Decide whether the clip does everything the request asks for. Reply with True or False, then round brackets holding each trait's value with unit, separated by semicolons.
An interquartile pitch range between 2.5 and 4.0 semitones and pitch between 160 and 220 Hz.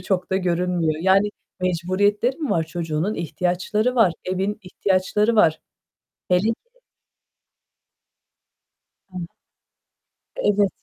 True (2.9 semitones; 185 Hz)